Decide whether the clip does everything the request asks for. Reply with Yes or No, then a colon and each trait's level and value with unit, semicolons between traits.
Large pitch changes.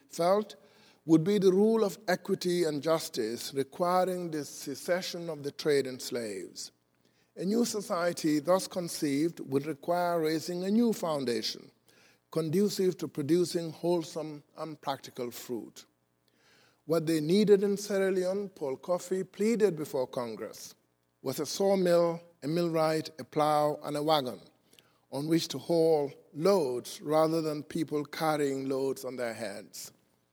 No: average, 4.6 semitones